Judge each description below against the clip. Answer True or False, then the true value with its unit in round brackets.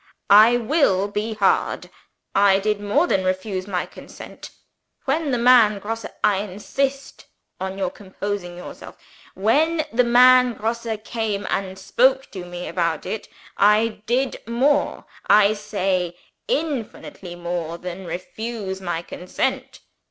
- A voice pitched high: True (205 Hz)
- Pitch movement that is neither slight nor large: True (4.2 semitones)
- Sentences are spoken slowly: True (130 wpm)